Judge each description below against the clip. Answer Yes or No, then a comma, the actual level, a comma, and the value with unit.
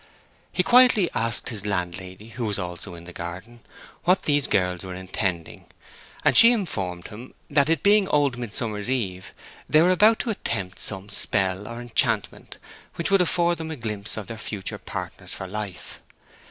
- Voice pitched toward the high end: No, low, 110 Hz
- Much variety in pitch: Yes, wide, 8.9 semitones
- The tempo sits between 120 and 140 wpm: No, average, 170 wpm